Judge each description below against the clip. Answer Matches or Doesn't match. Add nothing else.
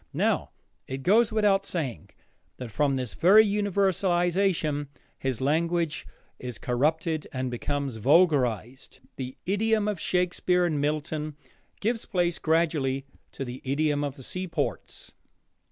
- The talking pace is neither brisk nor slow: Doesn't match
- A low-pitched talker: Doesn't match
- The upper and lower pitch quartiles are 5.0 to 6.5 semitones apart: Matches